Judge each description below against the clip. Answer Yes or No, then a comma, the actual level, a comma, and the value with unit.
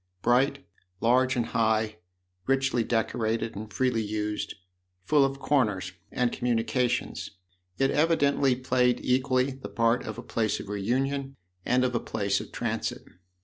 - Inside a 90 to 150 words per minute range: Yes, average, 145 wpm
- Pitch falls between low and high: No, low, 125 Hz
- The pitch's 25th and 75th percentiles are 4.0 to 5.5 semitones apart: No, average, 3.0 semitones